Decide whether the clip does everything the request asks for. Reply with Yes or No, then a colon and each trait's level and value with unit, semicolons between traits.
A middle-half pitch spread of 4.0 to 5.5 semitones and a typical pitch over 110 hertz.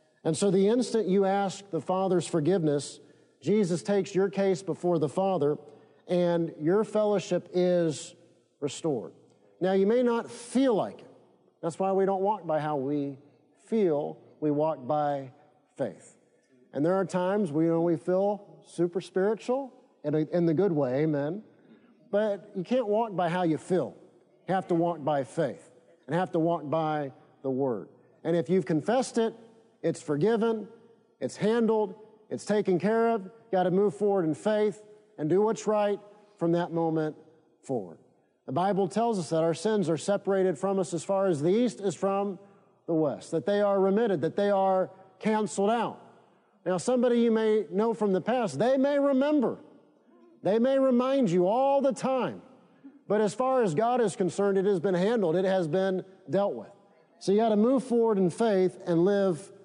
Yes: average, 4.4 semitones; high, 190 Hz